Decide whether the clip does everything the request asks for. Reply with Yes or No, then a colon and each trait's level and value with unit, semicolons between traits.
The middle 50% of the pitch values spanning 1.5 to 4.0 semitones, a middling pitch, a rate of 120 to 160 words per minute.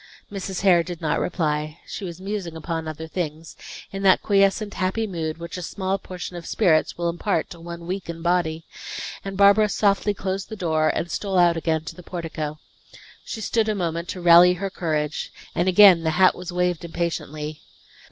No: average, 2.9 semitones; medium, 175 Hz; average, 190 wpm